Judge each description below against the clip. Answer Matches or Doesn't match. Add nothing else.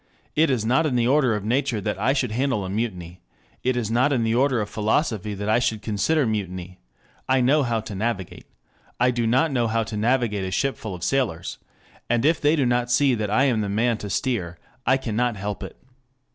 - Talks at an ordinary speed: Doesn't match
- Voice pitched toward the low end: Matches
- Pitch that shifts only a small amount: Doesn't match